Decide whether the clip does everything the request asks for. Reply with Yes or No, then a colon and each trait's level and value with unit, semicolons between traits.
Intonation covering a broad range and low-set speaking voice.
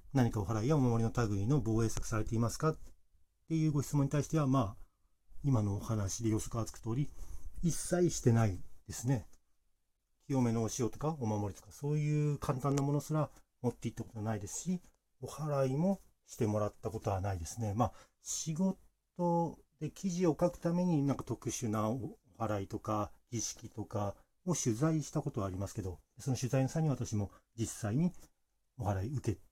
Yes: wide, 5.8 semitones; low, 115 Hz